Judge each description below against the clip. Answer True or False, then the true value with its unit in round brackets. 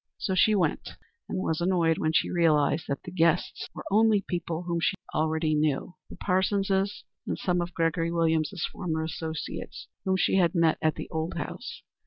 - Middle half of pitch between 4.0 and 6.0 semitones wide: False (2.7 semitones)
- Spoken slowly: False (180 wpm)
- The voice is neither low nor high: True (170 Hz)